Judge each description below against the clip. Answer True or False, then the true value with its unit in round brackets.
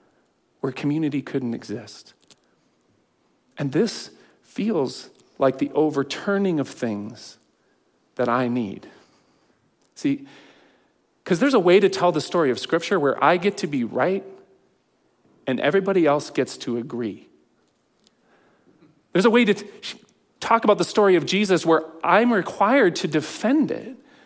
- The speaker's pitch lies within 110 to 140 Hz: False (175 Hz)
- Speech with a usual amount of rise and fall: False (7.5 semitones)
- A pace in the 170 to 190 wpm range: False (135 wpm)